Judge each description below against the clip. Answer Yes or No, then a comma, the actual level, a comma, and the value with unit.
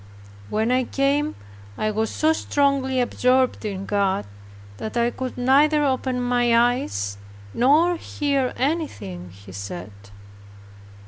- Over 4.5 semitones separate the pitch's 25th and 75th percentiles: Yes, average, 5.2 semitones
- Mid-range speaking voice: No, very high, 250 Hz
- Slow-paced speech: Yes, slow, 120 wpm